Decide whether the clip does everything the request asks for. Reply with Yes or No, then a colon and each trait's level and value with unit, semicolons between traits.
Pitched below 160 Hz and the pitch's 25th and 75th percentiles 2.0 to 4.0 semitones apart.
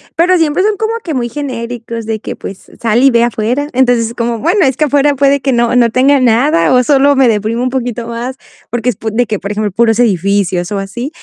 No: high, 240 Hz; average, 3.5 semitones